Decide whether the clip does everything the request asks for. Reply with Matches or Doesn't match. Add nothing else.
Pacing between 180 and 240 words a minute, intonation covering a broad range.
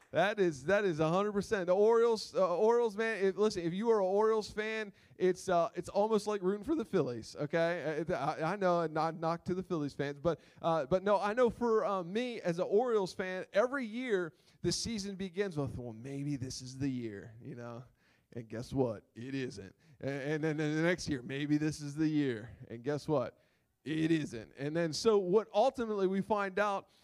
Matches